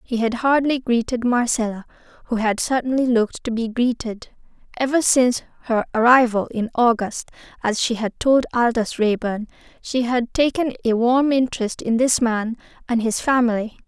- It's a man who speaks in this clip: No, female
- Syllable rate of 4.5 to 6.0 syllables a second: Yes, 5.0 syllables/s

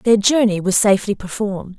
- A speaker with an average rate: Yes, average, 170 wpm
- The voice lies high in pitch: Yes, high, 205 Hz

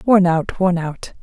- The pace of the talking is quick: No, average, 195 wpm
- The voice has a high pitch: No, medium, 180 Hz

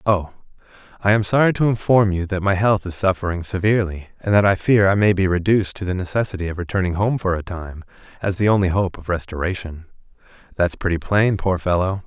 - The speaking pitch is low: Yes, very low, 95 Hz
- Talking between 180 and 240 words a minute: Yes, average, 200 wpm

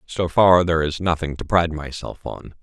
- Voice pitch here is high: No, very low, 80 Hz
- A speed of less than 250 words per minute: Yes, fast, 205 wpm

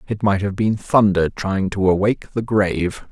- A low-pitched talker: Yes, low, 100 Hz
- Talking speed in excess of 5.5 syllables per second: No, 4.8 syllables/s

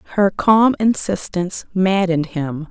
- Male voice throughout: No, female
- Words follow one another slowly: Yes, slow, 110 wpm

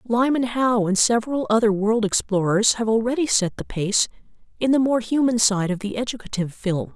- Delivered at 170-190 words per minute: Yes, average, 180 wpm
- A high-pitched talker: Yes, high, 225 Hz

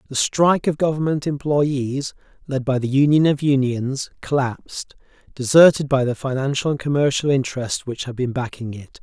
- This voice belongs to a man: Yes, male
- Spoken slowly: No, average, 160 wpm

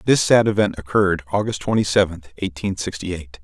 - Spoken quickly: No, average, 175 wpm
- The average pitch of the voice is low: Yes, very low, 95 Hz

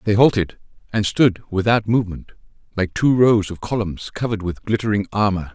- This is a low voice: Yes, low, 105 Hz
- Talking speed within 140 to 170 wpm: Yes, average, 160 wpm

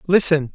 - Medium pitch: Yes, medium, 165 Hz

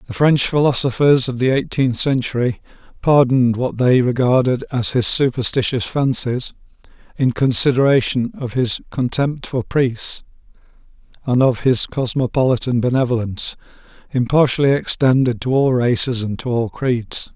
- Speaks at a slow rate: Yes, slow, 125 wpm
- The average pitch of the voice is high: No, low, 125 Hz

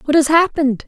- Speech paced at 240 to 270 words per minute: No, fast, 205 wpm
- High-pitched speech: Yes, very high, 295 Hz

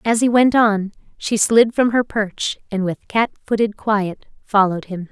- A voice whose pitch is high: Yes, high, 215 Hz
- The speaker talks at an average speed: Yes, average, 190 wpm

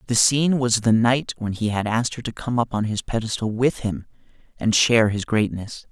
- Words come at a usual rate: No, fast, 225 wpm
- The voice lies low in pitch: Yes, low, 115 Hz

